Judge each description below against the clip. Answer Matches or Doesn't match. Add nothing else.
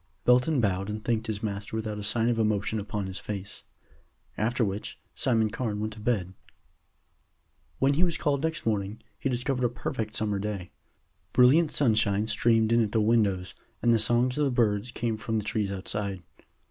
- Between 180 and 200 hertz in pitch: Doesn't match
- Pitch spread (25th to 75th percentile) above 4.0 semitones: Doesn't match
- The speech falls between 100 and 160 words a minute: Doesn't match